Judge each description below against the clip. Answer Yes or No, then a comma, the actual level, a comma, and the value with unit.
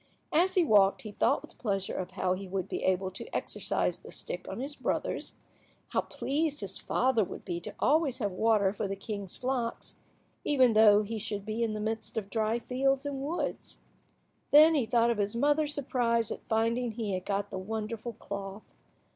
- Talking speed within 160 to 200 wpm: Yes, average, 195 wpm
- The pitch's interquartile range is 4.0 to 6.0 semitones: Yes, average, 4.5 semitones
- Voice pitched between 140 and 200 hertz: No, high, 225 Hz